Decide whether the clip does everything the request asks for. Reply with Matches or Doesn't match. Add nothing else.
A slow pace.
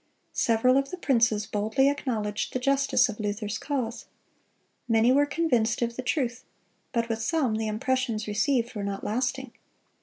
Doesn't match